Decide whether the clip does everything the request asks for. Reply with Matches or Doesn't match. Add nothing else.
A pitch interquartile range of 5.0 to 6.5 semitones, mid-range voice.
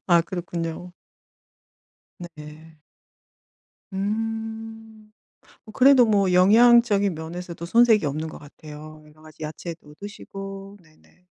Matches